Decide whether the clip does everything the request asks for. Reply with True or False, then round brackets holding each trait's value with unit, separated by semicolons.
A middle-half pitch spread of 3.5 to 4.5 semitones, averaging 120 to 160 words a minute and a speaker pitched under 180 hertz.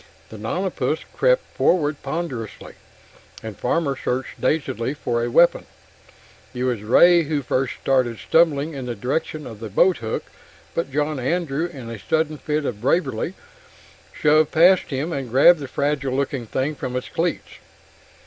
True (4.2 semitones; 150 wpm; 140 Hz)